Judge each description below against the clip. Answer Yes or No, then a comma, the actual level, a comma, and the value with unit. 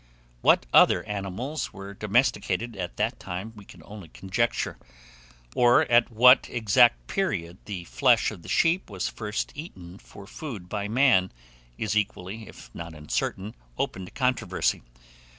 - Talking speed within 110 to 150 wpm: Yes, average, 145 wpm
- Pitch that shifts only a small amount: No, average, 4.3 semitones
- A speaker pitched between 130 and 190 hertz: No, low, 105 Hz